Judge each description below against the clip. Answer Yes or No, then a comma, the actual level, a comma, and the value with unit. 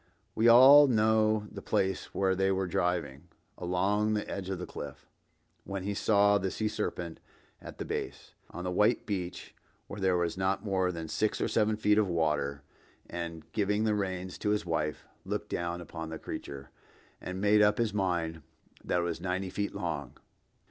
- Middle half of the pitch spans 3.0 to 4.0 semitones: Yes, average, 3.3 semitones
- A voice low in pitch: Yes, very low, 95 Hz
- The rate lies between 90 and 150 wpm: No, average, 175 wpm